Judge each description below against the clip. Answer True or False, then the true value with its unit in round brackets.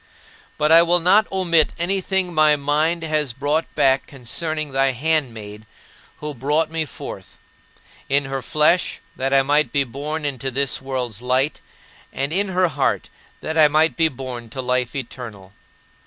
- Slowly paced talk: False (155 wpm)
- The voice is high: False (145 Hz)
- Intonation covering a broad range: False (3.4 semitones)